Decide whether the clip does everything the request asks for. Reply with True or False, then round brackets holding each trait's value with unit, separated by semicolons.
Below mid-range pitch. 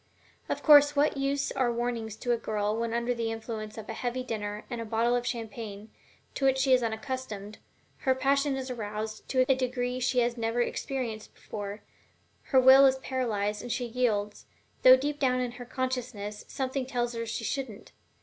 False (245 Hz)